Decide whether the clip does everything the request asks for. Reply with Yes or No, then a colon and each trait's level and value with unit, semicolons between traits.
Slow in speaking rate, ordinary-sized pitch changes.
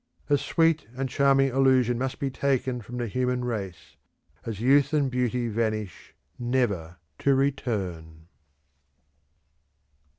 Yes: slow, 120 wpm; average, 3.7 semitones